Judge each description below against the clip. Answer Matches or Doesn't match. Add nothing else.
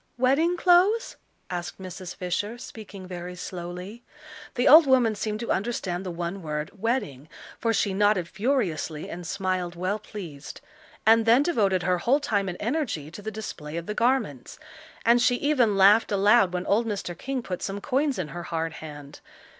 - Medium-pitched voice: Doesn't match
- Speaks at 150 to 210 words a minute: Matches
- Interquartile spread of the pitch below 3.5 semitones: Doesn't match